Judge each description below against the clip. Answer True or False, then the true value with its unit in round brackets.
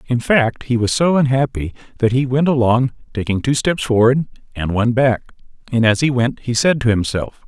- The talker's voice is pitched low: True (125 Hz)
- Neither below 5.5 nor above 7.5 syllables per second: False (5.3 syllables/s)